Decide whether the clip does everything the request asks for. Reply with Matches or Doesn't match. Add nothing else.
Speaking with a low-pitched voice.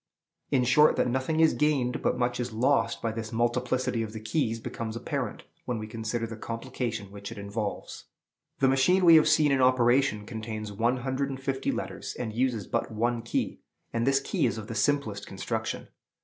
Matches